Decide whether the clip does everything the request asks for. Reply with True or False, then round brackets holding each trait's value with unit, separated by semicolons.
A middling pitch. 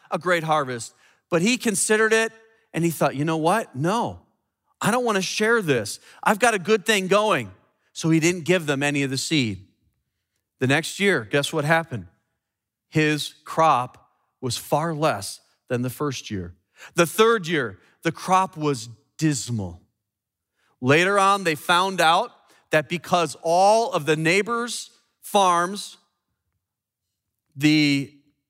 True (160 Hz)